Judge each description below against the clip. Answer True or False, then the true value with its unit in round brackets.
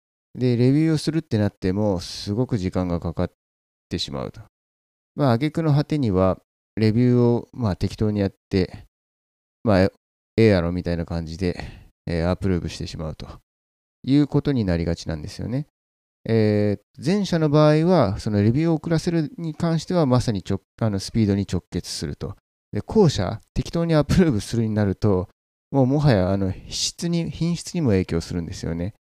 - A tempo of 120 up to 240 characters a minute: False (355 characters per minute)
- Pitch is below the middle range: True (100 Hz)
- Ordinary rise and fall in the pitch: False (8.4 semitones)